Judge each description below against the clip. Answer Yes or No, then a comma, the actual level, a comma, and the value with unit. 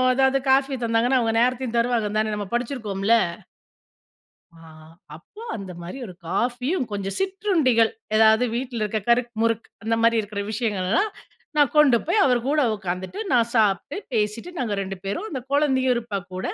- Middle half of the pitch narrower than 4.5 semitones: Yes, average, 3.8 semitones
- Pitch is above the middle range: Yes, high, 235 Hz